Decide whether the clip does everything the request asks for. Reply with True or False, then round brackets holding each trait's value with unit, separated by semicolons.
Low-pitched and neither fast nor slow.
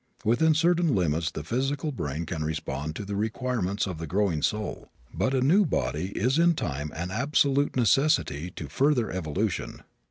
True (105 Hz; 165 wpm)